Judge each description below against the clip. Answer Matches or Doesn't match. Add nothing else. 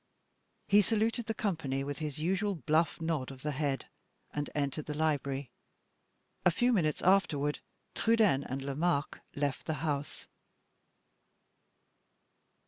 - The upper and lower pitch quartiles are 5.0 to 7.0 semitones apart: Doesn't match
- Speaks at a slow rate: Matches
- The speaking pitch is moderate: Matches